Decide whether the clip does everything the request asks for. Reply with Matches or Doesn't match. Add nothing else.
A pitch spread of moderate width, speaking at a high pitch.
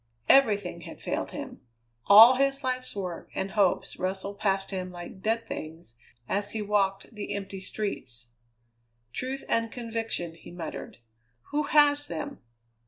Matches